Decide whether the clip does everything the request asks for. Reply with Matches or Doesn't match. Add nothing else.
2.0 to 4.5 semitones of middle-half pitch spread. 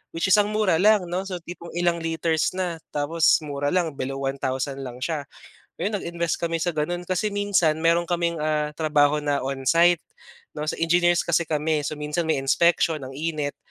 Matches